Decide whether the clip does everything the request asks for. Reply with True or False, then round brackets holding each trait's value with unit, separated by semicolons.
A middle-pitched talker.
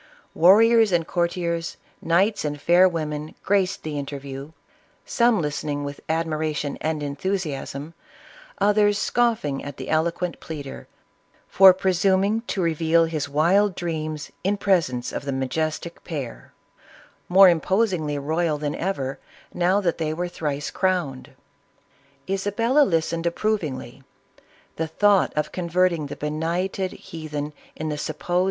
True (165 Hz)